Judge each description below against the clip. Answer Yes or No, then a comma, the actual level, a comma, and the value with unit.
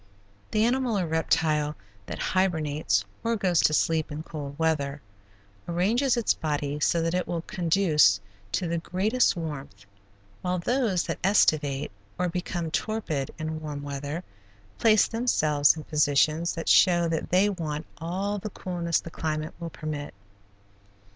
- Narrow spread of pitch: No, average, 3.6 semitones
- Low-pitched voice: No, medium, 165 Hz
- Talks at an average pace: Yes, average, 145 wpm